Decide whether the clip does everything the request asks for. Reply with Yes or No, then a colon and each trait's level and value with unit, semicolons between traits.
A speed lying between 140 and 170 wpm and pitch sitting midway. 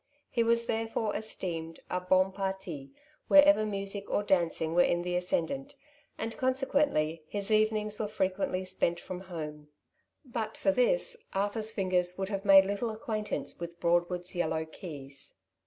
No: average, 150 wpm; high, 195 Hz